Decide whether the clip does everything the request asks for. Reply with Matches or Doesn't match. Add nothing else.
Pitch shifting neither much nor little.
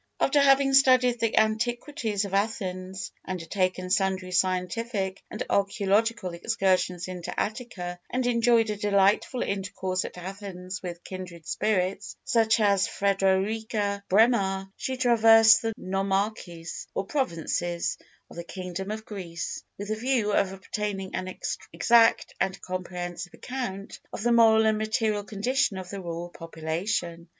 Matches